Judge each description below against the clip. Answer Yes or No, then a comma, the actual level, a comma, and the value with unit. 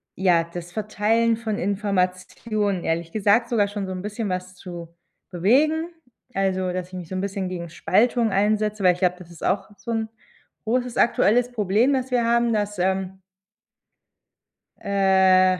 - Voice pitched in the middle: No, high, 200 Hz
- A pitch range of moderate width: Yes, average, 3.4 semitones